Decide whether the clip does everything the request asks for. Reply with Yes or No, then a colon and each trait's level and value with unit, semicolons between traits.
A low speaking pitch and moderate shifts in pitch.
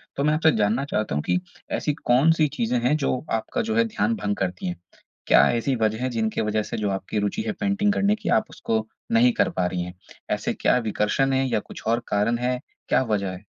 No: low, 120 Hz; wide, 6.5 semitones